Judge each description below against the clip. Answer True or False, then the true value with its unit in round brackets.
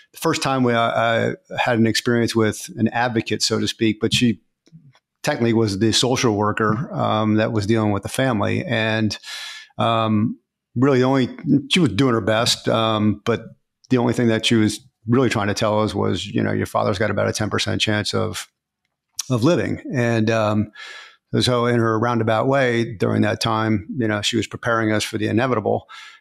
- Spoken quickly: False (190 wpm)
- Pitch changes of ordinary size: False (1.9 semitones)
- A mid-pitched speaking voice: False (115 Hz)